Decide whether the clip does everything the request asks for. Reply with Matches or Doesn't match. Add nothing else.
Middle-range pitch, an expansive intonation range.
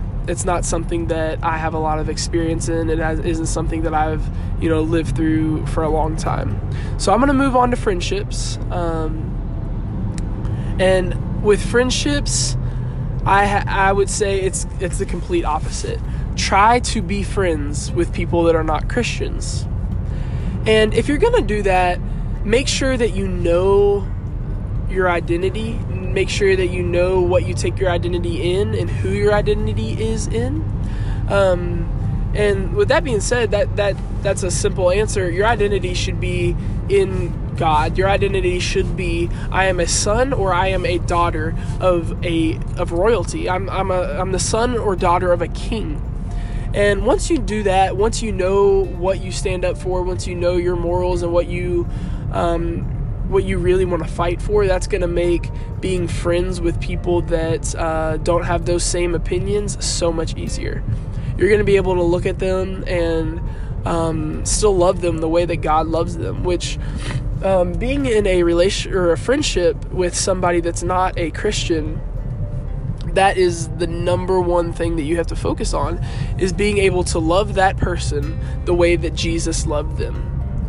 Matches